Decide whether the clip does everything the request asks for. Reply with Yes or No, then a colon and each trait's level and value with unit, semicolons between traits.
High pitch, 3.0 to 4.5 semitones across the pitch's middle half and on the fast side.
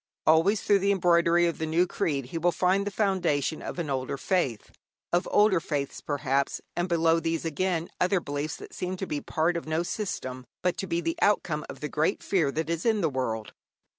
No: medium, 165 Hz; average, 3.4 semitones; fast, 210 wpm